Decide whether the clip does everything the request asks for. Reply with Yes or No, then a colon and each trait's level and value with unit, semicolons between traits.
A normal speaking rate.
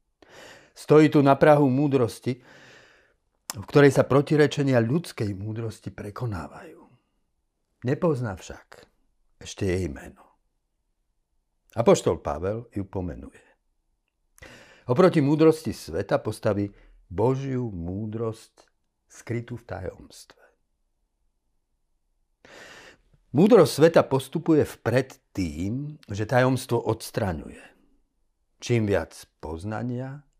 No: slow, 80 wpm